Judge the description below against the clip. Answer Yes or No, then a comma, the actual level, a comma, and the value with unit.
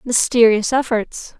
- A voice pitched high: Yes, high, 235 Hz